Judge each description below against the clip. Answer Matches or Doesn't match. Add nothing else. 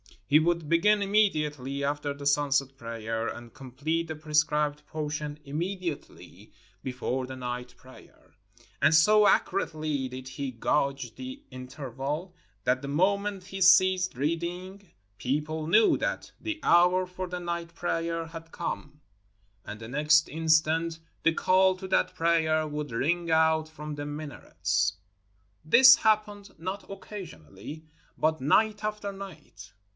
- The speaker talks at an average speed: Doesn't match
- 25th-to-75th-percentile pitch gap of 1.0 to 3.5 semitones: Doesn't match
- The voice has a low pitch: Doesn't match